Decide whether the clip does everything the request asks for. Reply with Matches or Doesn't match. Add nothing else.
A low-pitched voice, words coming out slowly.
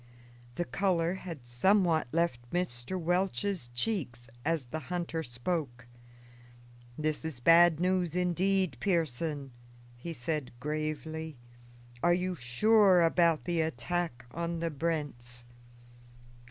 Doesn't match